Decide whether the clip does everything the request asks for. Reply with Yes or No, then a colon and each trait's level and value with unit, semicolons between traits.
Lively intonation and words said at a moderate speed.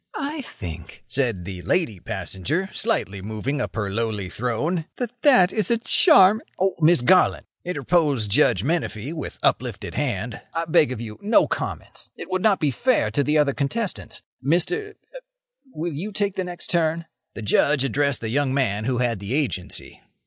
Yes: wide, 8.5 semitones; average, 170 wpm